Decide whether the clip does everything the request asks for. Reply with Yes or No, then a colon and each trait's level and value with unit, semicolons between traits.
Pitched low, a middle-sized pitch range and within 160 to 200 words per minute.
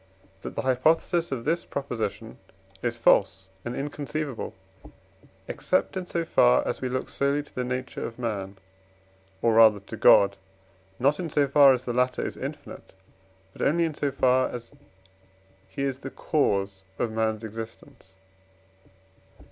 No: low, 125 Hz; average, 4.2 semitones; average, 150 wpm